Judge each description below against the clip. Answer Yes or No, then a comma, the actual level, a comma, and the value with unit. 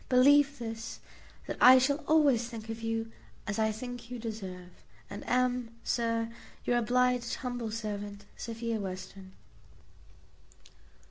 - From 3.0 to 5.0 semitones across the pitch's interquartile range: No, narrow, 2.4 semitones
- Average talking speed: No, slow, 125 wpm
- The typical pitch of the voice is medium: No, high, 230 Hz